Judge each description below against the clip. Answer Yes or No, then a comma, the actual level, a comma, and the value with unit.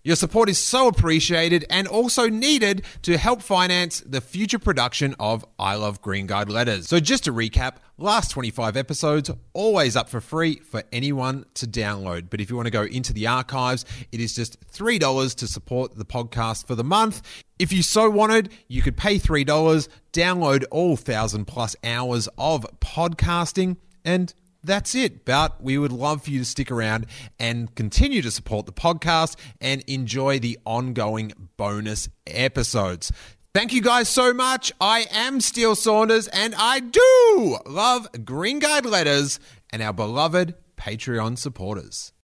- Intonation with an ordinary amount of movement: No, wide, 8.0 semitones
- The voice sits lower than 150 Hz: Yes, low, 135 Hz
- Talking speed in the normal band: Yes, average, 165 wpm